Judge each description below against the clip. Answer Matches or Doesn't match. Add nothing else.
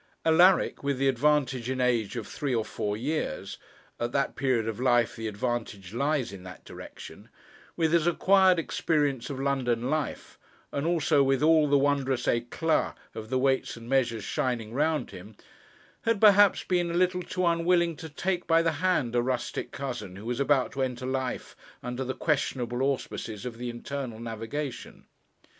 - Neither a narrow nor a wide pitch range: Matches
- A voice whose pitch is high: Doesn't match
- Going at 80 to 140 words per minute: Doesn't match